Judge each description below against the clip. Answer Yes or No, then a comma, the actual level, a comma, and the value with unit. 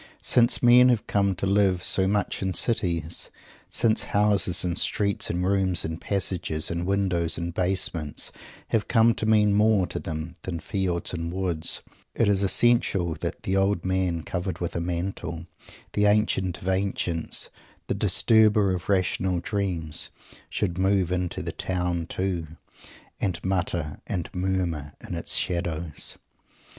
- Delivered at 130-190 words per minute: Yes, average, 150 wpm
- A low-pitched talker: Yes, very low, 95 Hz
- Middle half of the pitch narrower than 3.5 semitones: Yes, narrow, 2.6 semitones